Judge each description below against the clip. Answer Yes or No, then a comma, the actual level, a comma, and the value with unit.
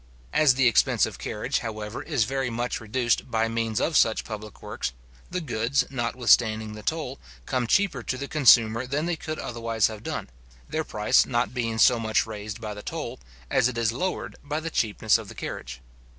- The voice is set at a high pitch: No, low, 115 Hz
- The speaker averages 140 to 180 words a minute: No, average, 195 wpm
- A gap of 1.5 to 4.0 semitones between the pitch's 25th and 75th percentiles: Yes, average, 3.3 semitones